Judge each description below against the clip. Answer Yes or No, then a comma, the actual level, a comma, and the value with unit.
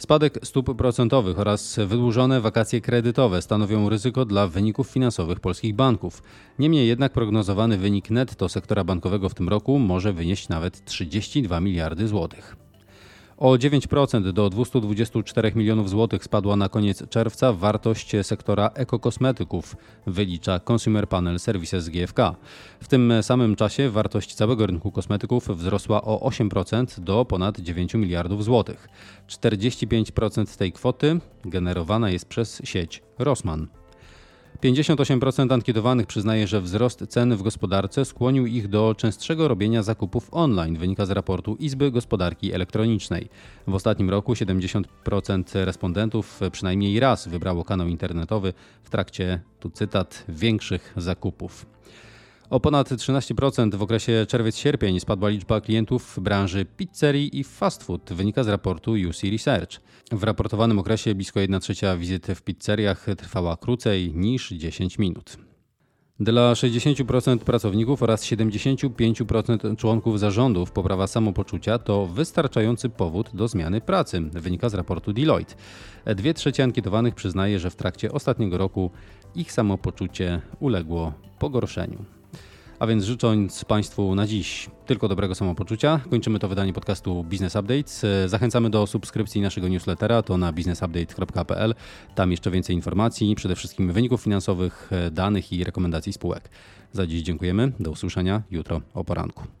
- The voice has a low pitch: Yes, low, 105 Hz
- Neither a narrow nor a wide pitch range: Yes, average, 3.9 semitones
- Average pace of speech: Yes, average, 130 wpm